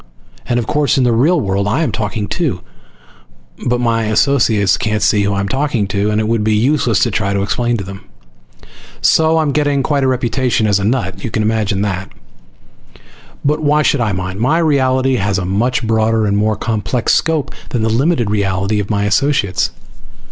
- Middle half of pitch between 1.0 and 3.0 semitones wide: No, average, 4.6 semitones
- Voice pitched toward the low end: Yes, low, 110 Hz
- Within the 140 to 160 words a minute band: No, average, 195 wpm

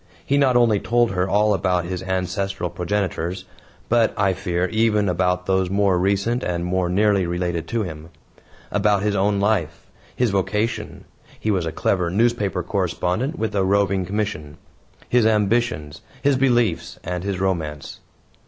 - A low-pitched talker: Yes, very low, 95 Hz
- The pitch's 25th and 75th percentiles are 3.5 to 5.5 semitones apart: No, average, 3.0 semitones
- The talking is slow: No, average, 155 wpm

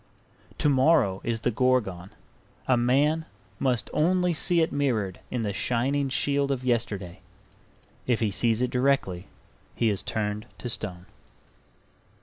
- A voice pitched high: No, low, 125 Hz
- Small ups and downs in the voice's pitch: No, average, 4.8 semitones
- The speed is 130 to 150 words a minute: Yes, slow, 135 wpm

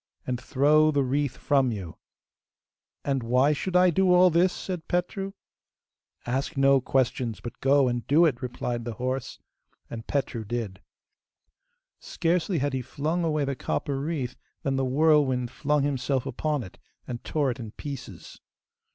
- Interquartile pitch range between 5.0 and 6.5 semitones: No, average, 3.6 semitones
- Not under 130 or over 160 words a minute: Yes, average, 155 wpm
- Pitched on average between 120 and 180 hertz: Yes, low, 135 Hz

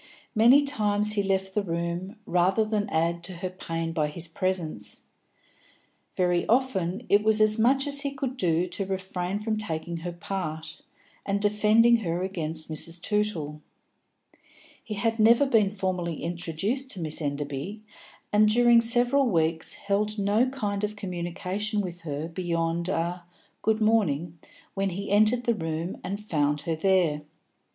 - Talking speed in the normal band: Yes, average, 150 wpm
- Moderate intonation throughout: Yes, average, 4.2 semitones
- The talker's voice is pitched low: No, high, 190 Hz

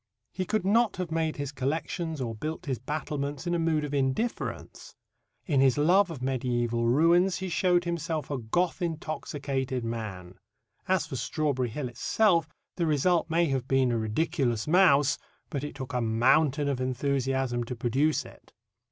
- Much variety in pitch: No, average, 4.4 semitones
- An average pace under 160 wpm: No, average, 165 wpm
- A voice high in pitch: No, medium, 145 Hz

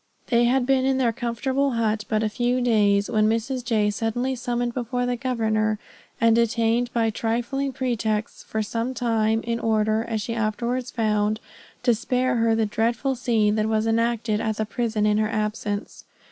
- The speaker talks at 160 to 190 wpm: Yes, average, 180 wpm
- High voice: Yes, high, 230 Hz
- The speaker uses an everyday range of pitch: No, narrow, 2.1 semitones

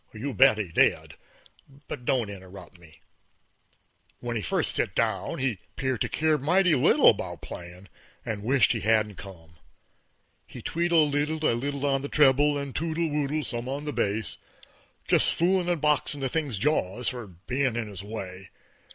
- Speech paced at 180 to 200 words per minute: No, average, 170 wpm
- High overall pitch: No, low, 130 Hz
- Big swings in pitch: Yes, wide, 6.3 semitones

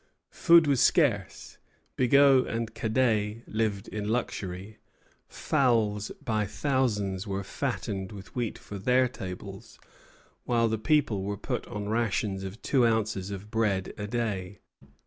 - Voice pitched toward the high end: No, low, 110 Hz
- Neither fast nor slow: No, slow, 130 wpm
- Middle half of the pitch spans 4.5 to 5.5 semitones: No, average, 3.1 semitones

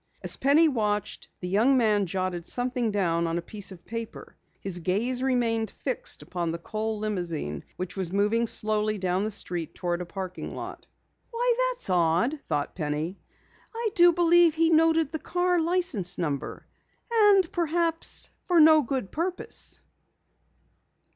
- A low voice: No, high, 220 Hz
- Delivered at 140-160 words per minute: Yes, average, 155 wpm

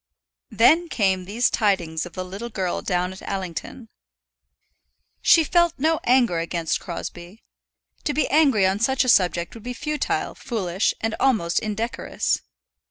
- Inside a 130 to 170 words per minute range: Yes, average, 145 wpm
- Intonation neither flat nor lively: No, wide, 5.9 semitones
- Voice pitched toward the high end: Yes, high, 210 Hz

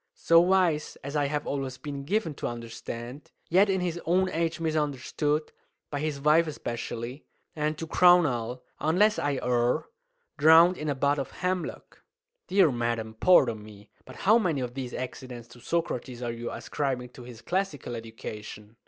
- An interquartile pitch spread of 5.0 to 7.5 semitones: Yes, wide, 5.4 semitones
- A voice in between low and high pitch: Yes, medium, 145 Hz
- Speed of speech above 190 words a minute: No, average, 165 wpm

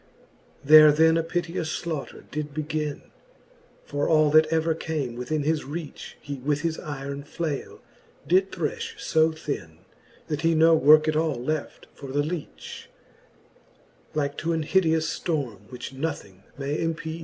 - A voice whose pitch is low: No, medium, 155 Hz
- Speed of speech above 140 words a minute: Yes, average, 150 wpm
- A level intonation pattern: Yes, narrow, 2.2 semitones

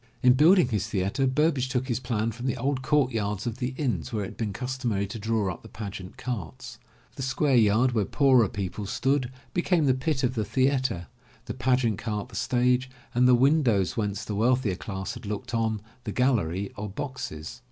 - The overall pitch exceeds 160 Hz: No, low, 120 Hz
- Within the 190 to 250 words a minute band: Yes, average, 200 wpm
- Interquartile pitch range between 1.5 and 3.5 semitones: No, average, 4.0 semitones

